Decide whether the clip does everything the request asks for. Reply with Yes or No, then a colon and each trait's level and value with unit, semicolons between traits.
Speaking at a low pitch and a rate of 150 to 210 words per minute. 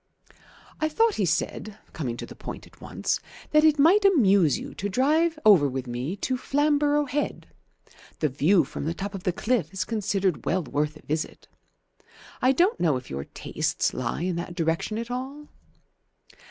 No: high, 200 Hz; average, 180 wpm